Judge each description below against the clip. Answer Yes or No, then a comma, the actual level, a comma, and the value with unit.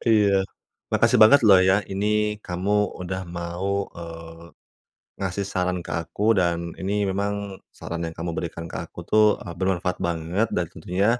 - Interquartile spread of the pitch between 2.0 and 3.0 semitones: Yes, narrow, 2.5 semitones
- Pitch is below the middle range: Yes, very low, 90 Hz